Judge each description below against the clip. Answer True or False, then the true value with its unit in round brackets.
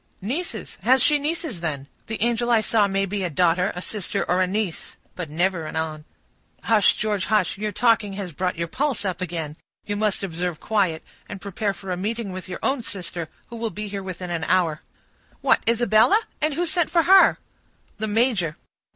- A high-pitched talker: True (200 Hz)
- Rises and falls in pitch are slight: False (4.3 semitones)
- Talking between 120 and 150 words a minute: False (195 wpm)